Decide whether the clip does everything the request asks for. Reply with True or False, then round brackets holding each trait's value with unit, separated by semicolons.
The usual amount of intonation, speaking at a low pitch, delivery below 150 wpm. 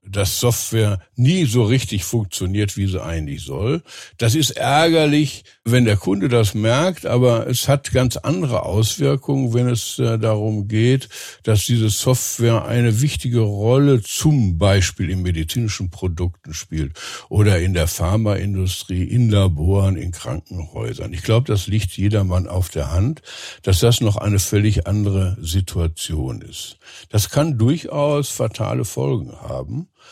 True (4.3 semitones; 110 Hz; 140 wpm)